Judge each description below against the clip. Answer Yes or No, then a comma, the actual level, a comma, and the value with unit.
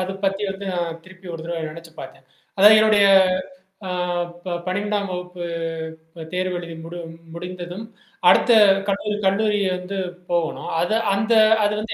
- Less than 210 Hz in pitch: Yes, medium, 185 Hz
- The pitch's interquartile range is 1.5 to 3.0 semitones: Yes, average, 2.7 semitones